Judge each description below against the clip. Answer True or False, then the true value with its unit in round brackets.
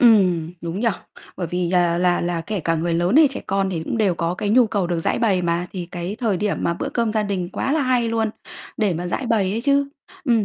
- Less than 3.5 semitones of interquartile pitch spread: False (4.5 semitones)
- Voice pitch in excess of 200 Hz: False (190 Hz)